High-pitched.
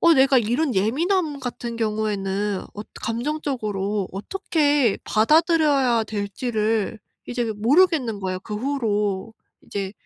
Yes: high, 230 Hz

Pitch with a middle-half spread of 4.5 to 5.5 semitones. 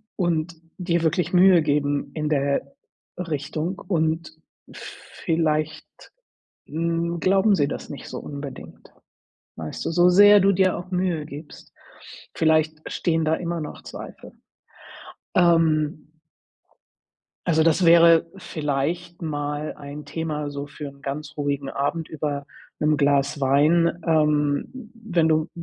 No: narrow, 2.6 semitones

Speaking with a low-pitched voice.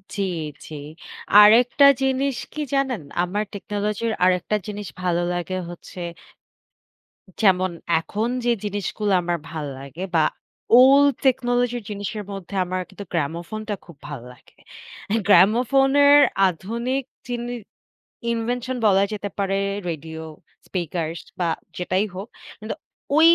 No: high, 205 Hz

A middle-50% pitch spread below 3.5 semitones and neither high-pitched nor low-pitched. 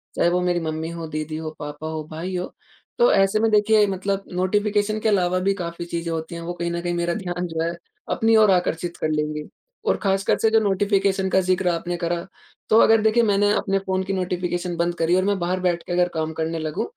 Yes: average, 2.8 semitones; medium, 180 Hz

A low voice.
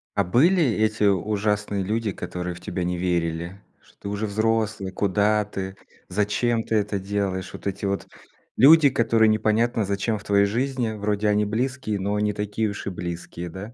Yes: low, 105 Hz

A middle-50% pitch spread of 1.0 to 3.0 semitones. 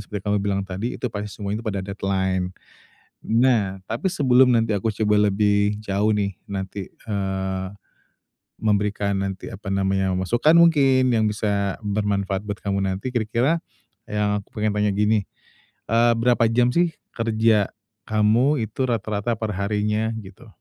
Yes: narrow, 2.5 semitones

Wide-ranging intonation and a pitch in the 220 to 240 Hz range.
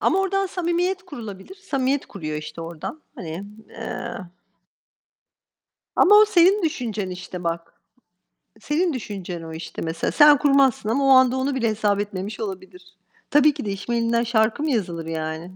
Yes: wide, 8.2 semitones; high, 230 Hz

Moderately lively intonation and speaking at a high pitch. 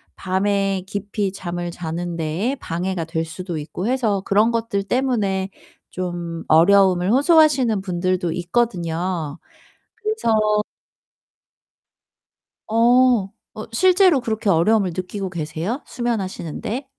Yes: average, 4.7 semitones; high, 195 Hz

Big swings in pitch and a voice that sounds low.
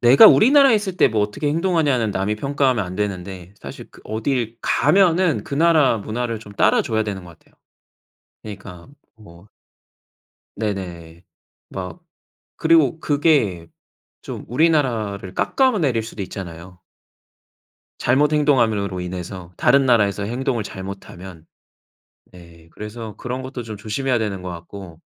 Yes: wide, 6.4 semitones; low, 110 Hz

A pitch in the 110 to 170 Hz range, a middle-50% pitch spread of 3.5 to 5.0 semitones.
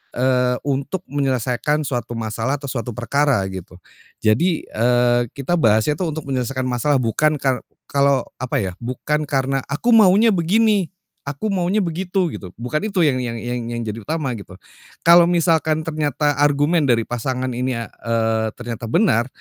Yes: low, 135 Hz; average, 4.7 semitones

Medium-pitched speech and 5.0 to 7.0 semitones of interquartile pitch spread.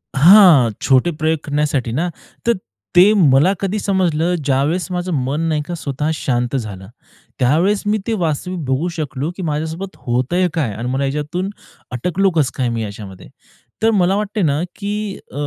Yes: medium, 155 Hz; wide, 5.5 semitones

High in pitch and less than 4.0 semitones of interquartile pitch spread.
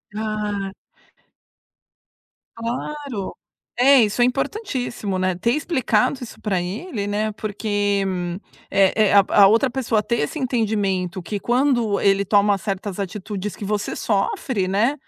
Yes: high, 210 Hz; average, 3.4 semitones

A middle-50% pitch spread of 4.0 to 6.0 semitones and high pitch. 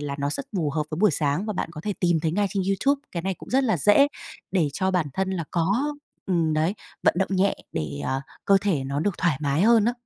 No: average, 4.8 semitones; medium, 180 Hz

